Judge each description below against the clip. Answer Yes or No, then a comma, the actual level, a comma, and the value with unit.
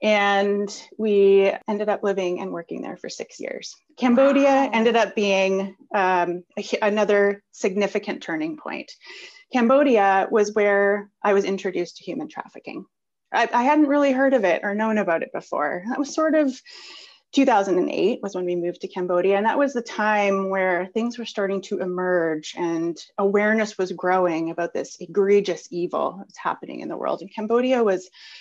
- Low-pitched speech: No, high, 205 Hz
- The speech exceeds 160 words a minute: Yes, average, 170 wpm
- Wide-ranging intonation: No, average, 3.9 semitones